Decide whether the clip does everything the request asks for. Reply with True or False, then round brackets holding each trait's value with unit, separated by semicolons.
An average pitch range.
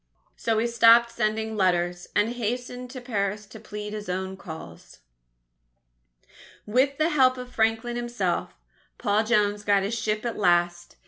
True (3.2 semitones)